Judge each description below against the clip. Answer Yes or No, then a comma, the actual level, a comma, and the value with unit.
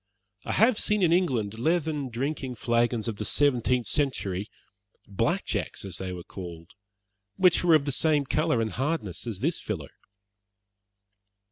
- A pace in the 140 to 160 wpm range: Yes, average, 150 wpm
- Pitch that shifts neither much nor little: No, wide, 6.9 semitones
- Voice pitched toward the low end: Yes, low, 125 Hz